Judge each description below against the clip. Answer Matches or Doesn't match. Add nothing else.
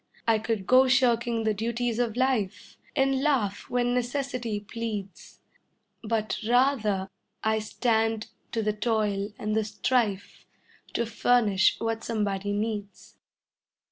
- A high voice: Matches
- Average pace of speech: Doesn't match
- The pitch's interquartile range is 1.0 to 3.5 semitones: Matches